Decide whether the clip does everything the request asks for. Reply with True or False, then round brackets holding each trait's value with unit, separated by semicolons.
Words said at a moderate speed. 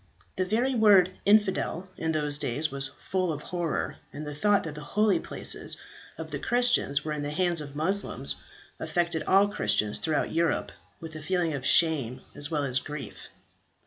True (180 wpm)